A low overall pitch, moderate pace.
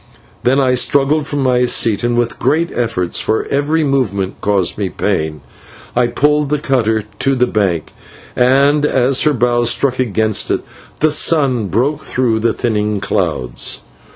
Yes: low, 125 Hz; average, 155 wpm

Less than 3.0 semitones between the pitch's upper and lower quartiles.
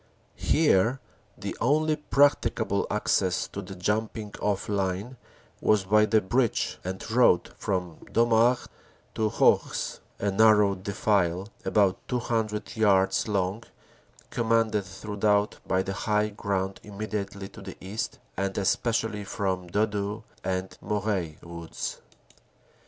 Yes: narrow, 2.5 semitones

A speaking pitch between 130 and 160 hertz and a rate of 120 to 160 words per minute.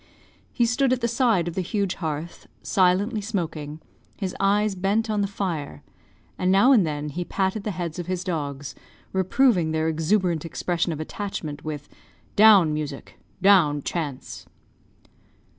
No: medium, 180 Hz; average, 150 wpm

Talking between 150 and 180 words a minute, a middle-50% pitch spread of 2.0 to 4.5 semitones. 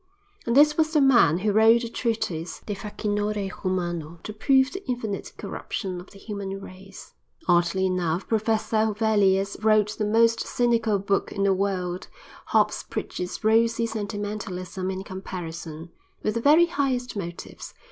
No: average, 140 wpm; average, 3.5 semitones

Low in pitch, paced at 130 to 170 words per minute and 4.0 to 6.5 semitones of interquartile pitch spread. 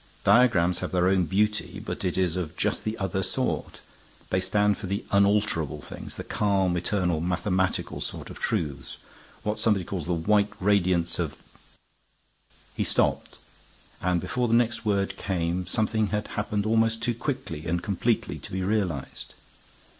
No: very low, 95 Hz; average, 160 wpm; average, 3.2 semitones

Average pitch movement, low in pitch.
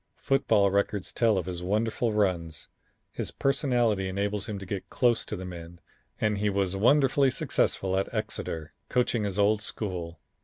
Yes: average, 3.1 semitones; low, 100 Hz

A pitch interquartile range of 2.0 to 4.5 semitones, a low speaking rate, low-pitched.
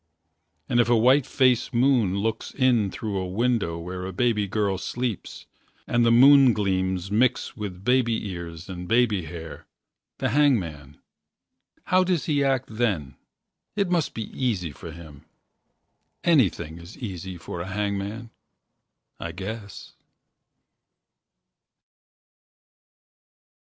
No: average, 5.2 semitones; slow, 120 wpm; low, 105 Hz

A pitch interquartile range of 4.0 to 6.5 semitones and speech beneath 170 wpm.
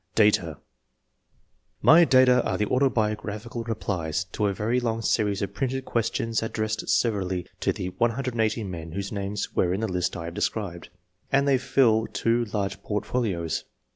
No: average, 3.3 semitones; average, 160 wpm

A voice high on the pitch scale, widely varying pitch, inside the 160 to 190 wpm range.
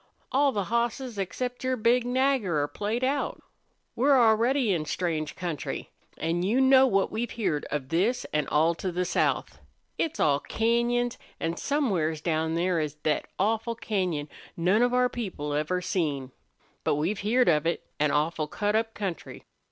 Yes: high, 195 Hz; wide, 6.9 semitones; average, 165 wpm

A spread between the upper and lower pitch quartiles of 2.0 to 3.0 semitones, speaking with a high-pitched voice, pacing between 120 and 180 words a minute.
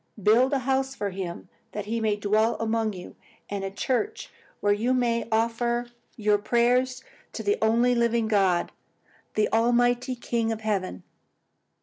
Yes: average, 2.7 semitones; high, 230 Hz; average, 150 wpm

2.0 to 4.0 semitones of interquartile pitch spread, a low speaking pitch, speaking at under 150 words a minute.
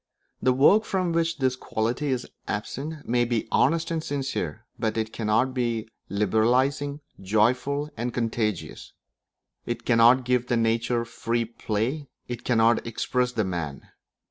Yes: average, 3.2 semitones; low, 120 Hz; average, 140 wpm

